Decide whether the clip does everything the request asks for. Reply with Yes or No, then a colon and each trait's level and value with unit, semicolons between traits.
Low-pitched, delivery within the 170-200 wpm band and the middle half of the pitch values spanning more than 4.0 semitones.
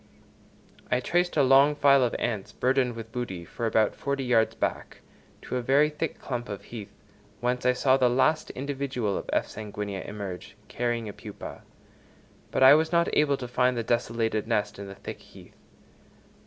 No: low, 125 Hz; average, 180 wpm; average, 3.6 semitones